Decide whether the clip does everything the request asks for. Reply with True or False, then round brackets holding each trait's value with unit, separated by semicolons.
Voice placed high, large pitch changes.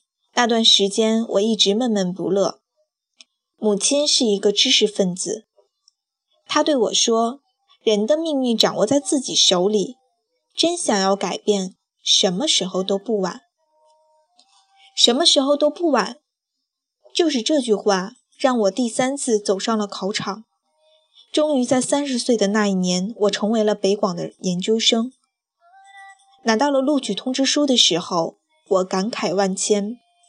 True (230 Hz; 6.6 semitones)